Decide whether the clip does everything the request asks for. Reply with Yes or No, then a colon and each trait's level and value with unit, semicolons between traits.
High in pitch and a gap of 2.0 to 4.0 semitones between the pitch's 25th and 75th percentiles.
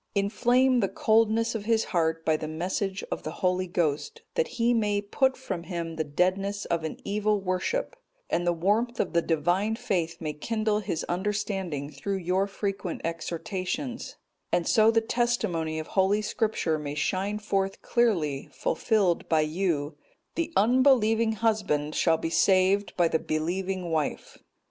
No: high, 195 Hz; average, 4.8 semitones